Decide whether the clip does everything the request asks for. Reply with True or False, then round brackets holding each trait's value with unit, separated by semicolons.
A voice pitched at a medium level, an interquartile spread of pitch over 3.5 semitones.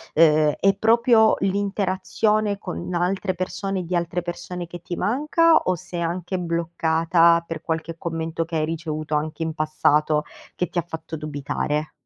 False (170 Hz; 2.7 semitones)